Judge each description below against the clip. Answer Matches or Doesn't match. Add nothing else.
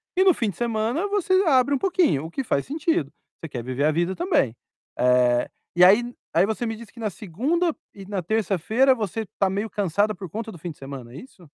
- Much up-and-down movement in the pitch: Matches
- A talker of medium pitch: Doesn't match